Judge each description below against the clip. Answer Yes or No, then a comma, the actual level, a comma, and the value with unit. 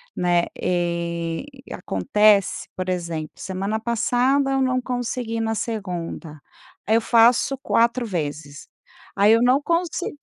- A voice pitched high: Yes, high, 215 Hz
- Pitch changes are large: Yes, wide, 6.0 semitones